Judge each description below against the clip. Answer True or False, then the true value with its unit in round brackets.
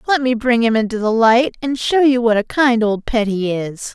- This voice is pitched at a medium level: False (235 Hz)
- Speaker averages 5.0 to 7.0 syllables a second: False (4.8 syllables/s)